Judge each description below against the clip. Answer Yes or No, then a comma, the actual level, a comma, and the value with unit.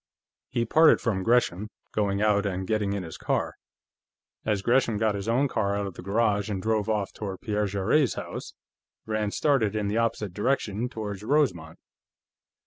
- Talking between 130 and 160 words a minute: No, average, 170 wpm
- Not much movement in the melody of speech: Yes, narrow, 2.3 semitones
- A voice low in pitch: Yes, low, 105 Hz